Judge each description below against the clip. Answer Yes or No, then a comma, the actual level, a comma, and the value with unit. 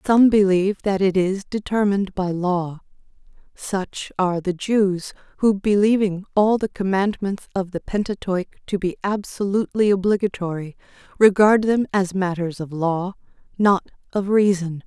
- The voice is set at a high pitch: Yes, high, 195 Hz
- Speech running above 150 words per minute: No, slow, 135 wpm